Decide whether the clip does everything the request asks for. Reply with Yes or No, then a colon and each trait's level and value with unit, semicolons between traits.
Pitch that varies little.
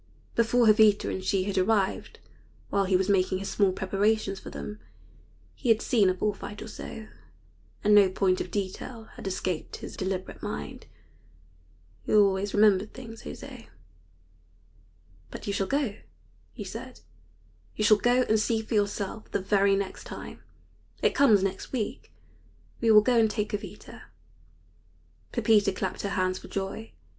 Yes: narrow, 2.3 semitones